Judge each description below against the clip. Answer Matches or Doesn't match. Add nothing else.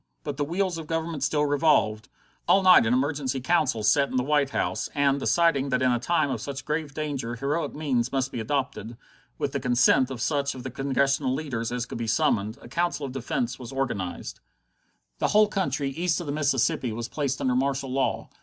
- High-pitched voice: Doesn't match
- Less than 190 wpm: Doesn't match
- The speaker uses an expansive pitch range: Doesn't match